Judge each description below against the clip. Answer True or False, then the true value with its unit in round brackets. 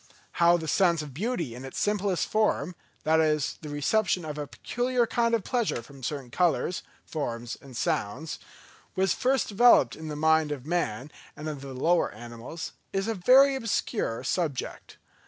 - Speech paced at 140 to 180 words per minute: True (160 wpm)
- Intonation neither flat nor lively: False (6.1 semitones)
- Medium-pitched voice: True (160 Hz)